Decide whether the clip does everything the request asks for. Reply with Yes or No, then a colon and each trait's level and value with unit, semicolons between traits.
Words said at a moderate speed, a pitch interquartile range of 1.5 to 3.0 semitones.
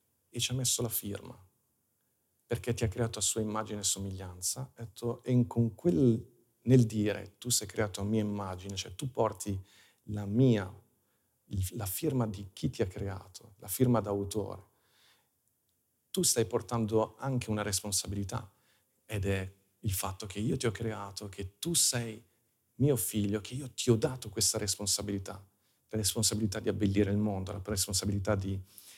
Yes: average, 160 wpm; average, 2.7 semitones